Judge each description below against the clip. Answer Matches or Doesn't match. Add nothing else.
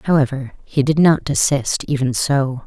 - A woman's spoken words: Matches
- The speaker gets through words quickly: Doesn't match